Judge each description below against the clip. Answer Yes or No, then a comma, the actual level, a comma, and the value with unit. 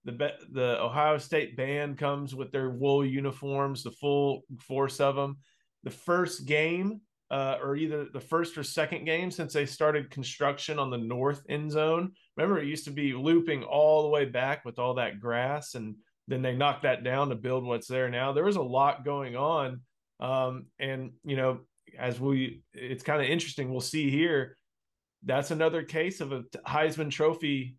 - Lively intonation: No, average, 2.8 semitones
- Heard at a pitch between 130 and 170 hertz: Yes, medium, 140 Hz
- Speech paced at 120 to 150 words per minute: No, average, 185 wpm